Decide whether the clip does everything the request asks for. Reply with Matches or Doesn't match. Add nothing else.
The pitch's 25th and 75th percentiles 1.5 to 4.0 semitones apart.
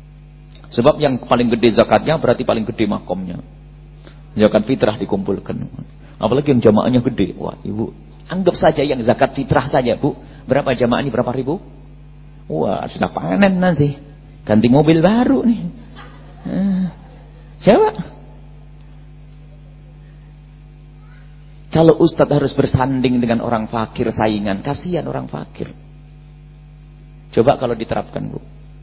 Matches